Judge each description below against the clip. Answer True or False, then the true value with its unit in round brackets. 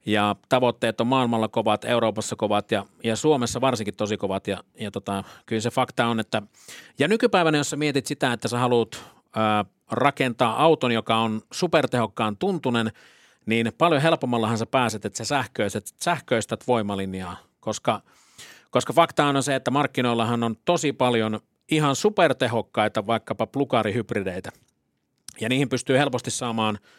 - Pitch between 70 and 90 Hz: False (120 Hz)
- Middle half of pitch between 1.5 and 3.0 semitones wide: False (3.6 semitones)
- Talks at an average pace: True (145 wpm)